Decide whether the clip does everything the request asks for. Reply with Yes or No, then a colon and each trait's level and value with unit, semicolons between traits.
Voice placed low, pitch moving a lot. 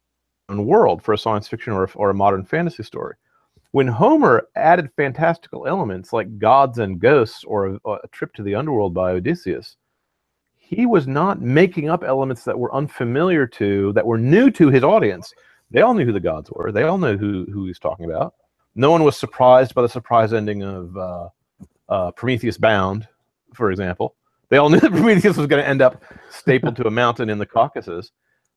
Yes: low, 115 Hz; wide, 5.7 semitones